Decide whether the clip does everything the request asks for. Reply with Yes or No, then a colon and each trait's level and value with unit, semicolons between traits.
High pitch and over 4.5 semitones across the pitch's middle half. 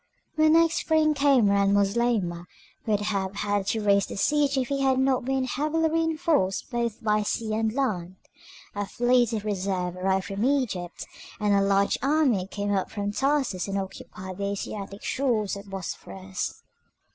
Yes: high, 210 Hz; wide, 5.4 semitones